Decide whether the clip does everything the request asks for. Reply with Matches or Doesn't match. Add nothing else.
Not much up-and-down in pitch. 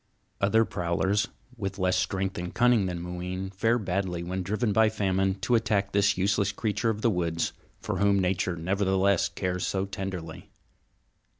Matches